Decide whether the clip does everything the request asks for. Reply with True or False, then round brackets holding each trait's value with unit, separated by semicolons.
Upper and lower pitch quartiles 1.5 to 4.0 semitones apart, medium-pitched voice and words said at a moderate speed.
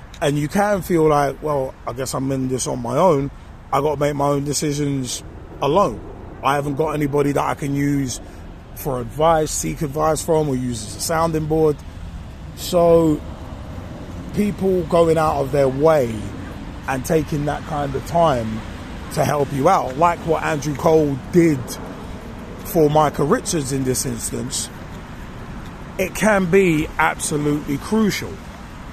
True (3.7 semitones; 145 Hz; 155 wpm)